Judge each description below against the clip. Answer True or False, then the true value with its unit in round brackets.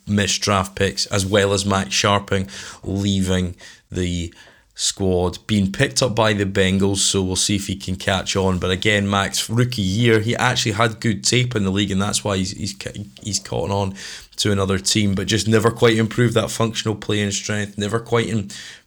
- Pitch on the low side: True (100 Hz)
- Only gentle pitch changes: True (2.3 semitones)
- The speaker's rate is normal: True (195 wpm)